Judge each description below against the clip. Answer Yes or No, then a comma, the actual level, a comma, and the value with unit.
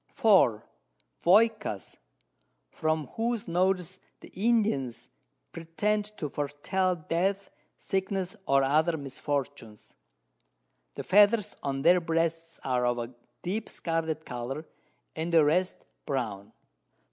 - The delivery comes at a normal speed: No, slow, 105 wpm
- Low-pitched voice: No, medium, 165 Hz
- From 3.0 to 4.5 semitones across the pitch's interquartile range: No, wide, 5.6 semitones